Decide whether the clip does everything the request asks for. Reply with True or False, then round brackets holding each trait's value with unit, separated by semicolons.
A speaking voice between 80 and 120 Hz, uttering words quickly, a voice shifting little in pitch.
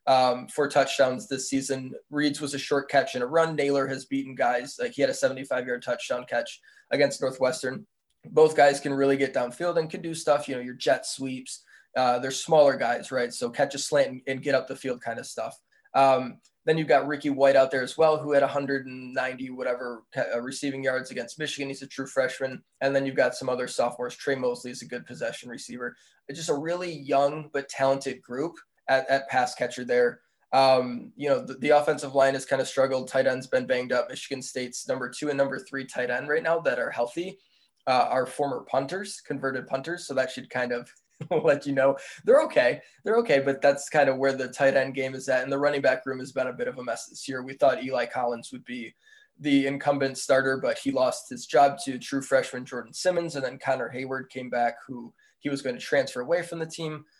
False (135 Hz; 225 wpm; 2.2 semitones)